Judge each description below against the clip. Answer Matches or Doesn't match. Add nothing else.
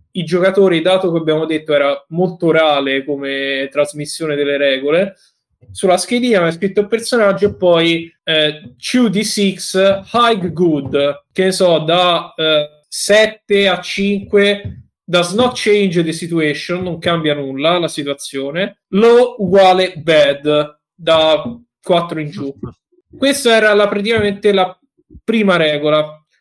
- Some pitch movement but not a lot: Matches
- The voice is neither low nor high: Matches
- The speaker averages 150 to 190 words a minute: Doesn't match